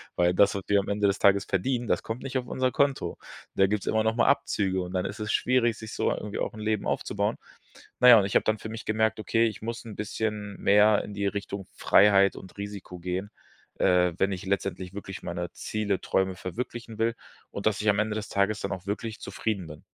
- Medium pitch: No, low, 105 Hz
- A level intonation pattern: Yes, narrow, 2.2 semitones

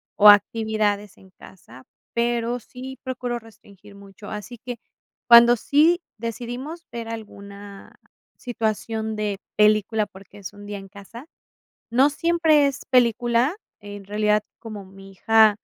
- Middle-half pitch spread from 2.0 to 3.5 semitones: Yes, average, 2.9 semitones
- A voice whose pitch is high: Yes, high, 220 Hz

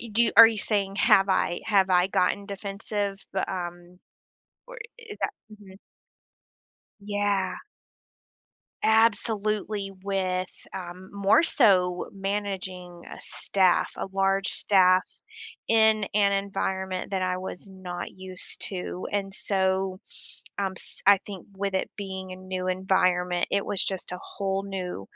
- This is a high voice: Yes, high, 195 Hz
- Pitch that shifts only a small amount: Yes, narrow, 1.6 semitones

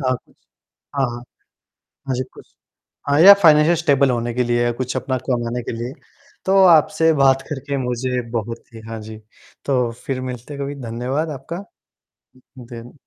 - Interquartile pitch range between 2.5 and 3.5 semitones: Yes, average, 2.9 semitones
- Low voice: Yes, low, 130 Hz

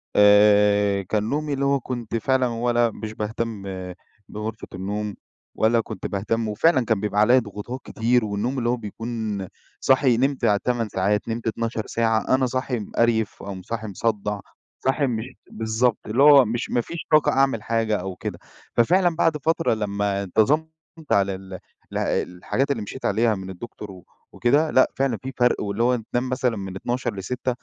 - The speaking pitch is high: No, low, 115 Hz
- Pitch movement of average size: Yes, average, 3.6 semitones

